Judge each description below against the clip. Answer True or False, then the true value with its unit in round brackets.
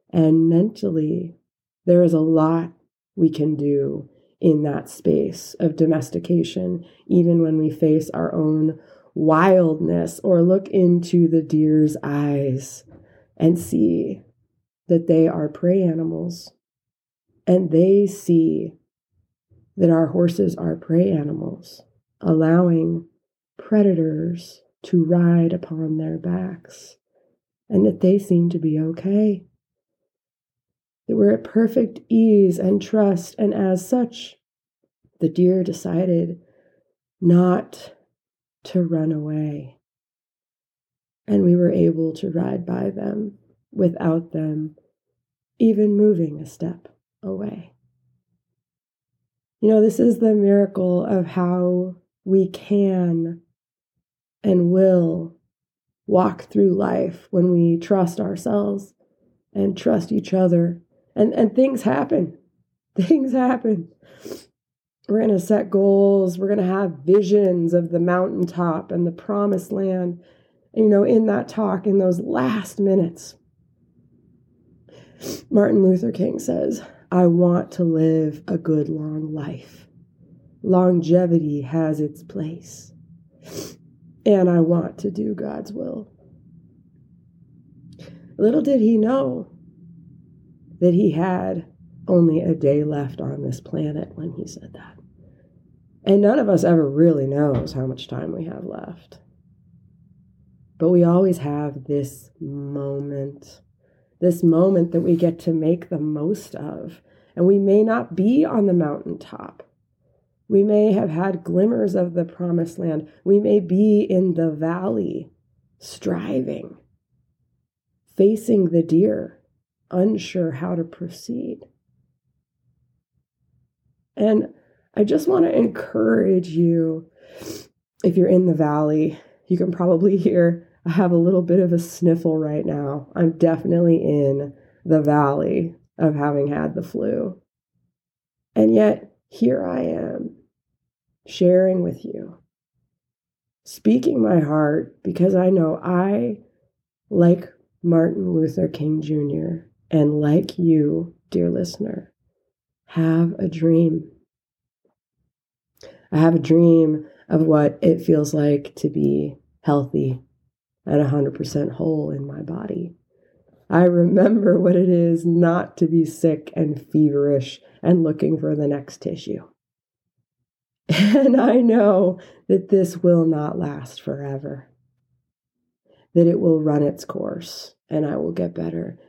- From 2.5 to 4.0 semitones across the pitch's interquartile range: True (3.2 semitones)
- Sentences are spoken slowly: True (120 wpm)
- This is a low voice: False (170 Hz)